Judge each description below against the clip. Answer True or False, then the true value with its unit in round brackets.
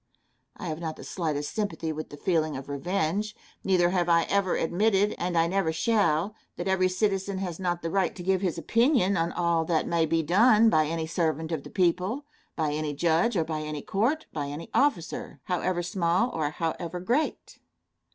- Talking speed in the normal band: True (190 wpm)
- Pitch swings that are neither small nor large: True (3.3 semitones)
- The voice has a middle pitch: True (175 Hz)